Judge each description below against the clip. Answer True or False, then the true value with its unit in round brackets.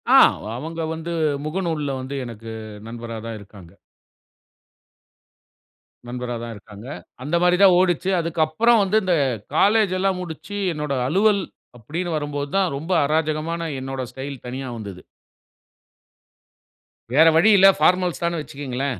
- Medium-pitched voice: True (155 Hz)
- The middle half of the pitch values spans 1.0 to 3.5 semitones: False (5.5 semitones)